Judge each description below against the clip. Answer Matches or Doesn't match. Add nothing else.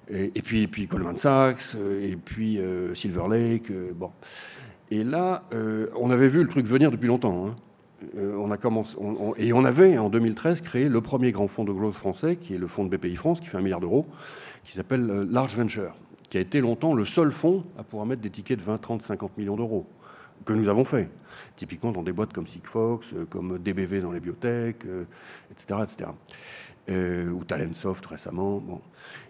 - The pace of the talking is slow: Doesn't match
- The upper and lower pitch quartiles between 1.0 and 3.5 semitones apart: Doesn't match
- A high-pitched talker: Doesn't match